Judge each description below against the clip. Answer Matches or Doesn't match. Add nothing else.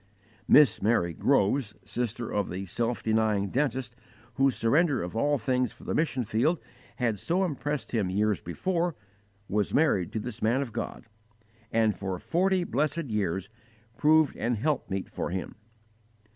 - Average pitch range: Doesn't match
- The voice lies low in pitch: Matches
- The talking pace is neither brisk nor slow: Matches